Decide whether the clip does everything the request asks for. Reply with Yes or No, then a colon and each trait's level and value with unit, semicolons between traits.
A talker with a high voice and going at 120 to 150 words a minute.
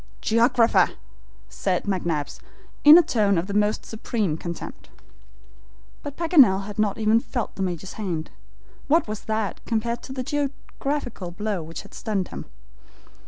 Yes: high, 215 Hz; average, 145 wpm